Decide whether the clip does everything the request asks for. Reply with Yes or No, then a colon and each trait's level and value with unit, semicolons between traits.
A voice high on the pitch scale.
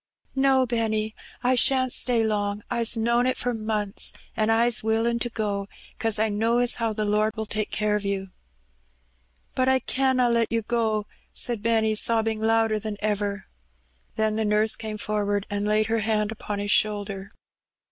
Yes: high, 220 Hz